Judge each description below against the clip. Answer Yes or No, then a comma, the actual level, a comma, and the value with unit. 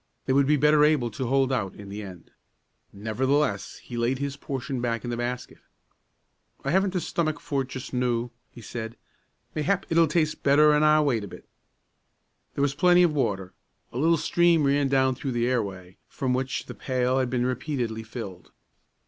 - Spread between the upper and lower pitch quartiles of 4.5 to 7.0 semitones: No, average, 3.9 semitones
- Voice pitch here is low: Yes, low, 130 Hz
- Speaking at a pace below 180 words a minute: No, average, 190 wpm